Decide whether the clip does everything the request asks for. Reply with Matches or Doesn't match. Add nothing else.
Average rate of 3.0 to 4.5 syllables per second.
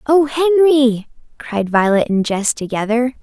Matches